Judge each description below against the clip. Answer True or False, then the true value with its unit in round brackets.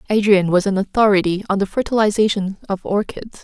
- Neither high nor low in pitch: False (200 Hz)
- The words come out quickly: False (155 wpm)